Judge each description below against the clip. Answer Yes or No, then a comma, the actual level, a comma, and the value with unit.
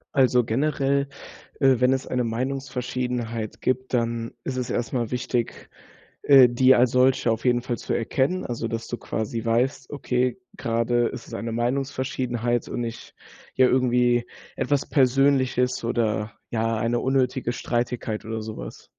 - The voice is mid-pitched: No, low, 125 Hz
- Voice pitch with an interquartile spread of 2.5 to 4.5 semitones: No, narrow, 2.0 semitones